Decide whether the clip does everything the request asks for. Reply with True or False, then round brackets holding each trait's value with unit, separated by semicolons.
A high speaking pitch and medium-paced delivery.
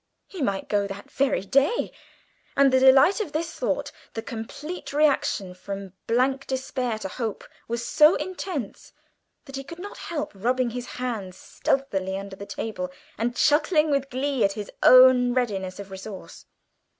True (250 Hz; 160 wpm)